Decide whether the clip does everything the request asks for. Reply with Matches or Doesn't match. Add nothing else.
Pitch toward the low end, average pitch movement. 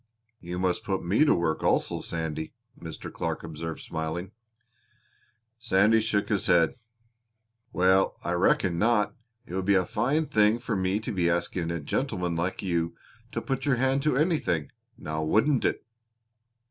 Matches